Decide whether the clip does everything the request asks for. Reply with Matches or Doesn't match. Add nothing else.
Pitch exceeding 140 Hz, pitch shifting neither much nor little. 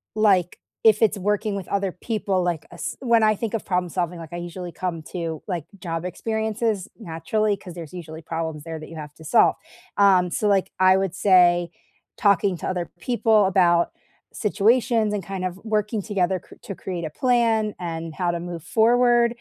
Matches